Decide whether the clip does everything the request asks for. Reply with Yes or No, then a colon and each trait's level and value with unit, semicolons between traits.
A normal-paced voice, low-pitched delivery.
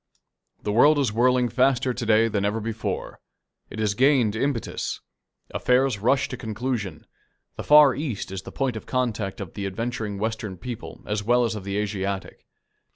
Yes: average, 170 wpm; low, 115 Hz